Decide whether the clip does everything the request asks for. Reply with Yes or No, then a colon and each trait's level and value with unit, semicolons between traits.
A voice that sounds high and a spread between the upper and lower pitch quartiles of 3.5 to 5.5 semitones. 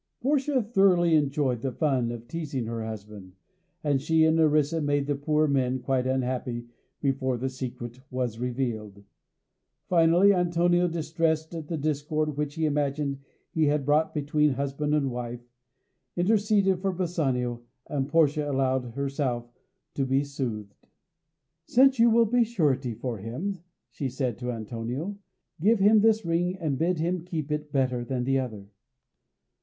No: medium, 145 Hz; average, 4.6 semitones